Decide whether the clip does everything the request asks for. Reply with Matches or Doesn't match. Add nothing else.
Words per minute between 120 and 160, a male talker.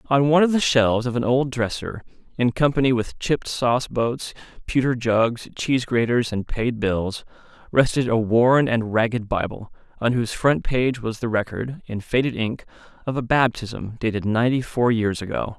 Doesn't match